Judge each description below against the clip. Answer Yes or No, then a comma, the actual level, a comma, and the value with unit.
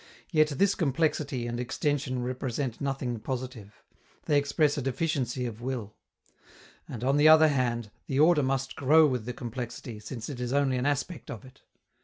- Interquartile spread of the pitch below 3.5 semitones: Yes, average, 3.1 semitones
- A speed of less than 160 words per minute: No, average, 170 wpm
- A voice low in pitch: Yes, low, 130 Hz